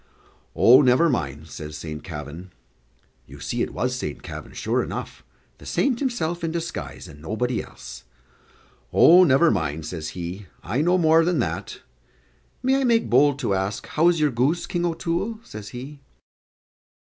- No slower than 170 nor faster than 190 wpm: No, average, 160 wpm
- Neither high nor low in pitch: No, low, 130 Hz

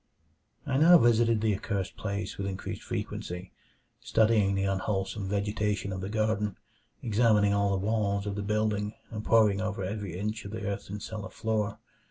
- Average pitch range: No, narrow, 1.7 semitones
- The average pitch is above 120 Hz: No, low, 105 Hz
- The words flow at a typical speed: Yes, average, 165 wpm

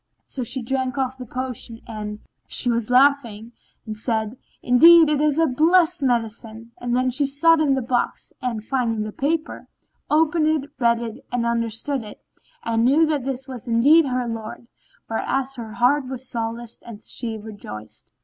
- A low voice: No, very high, 250 Hz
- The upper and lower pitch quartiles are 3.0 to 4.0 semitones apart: Yes, average, 3.5 semitones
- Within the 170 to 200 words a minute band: No, average, 160 wpm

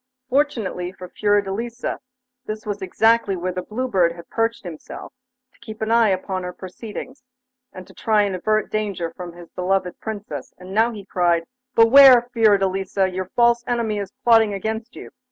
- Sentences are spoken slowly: No, average, 165 wpm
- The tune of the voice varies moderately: Yes, average, 3.6 semitones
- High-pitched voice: Yes, high, 205 Hz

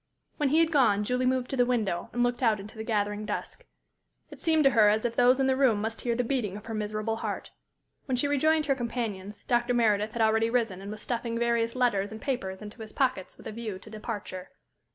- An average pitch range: Yes, average, 3.0 semitones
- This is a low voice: No, high, 230 Hz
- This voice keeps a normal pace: No, fast, 235 wpm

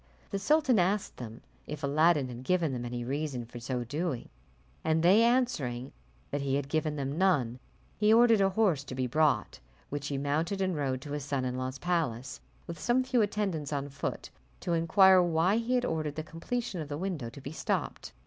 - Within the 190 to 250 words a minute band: Yes, average, 200 wpm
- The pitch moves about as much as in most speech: No, wide, 5.9 semitones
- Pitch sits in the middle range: Yes, medium, 155 Hz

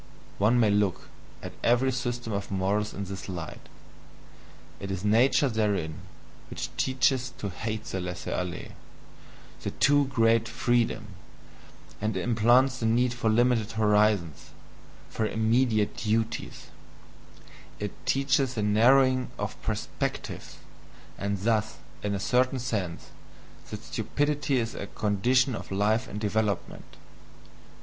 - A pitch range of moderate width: Yes, average, 3.4 semitones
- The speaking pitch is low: Yes, low, 110 Hz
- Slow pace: Yes, slow, 125 wpm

